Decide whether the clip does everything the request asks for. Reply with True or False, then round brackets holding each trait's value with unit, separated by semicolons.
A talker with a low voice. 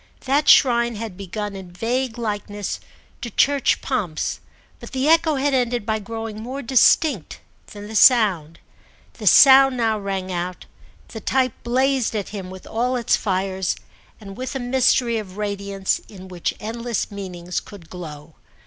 False (220 Hz)